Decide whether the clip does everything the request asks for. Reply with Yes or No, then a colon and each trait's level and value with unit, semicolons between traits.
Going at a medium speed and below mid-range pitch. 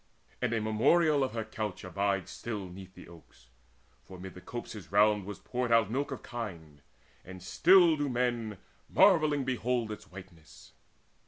Yes: average, 160 wpm; low, 110 Hz